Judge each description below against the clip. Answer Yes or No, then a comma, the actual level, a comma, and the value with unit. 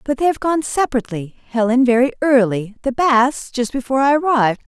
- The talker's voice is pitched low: No, very high, 255 Hz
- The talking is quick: No, average, 165 wpm